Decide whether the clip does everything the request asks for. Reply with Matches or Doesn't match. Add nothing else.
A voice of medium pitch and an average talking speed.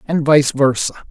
Matches